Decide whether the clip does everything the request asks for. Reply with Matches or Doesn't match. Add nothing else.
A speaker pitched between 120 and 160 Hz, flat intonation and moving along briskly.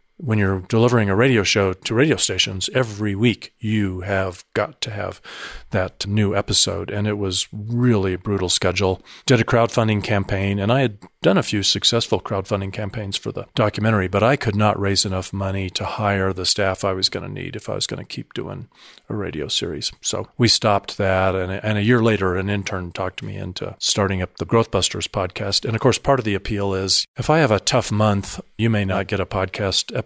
Doesn't match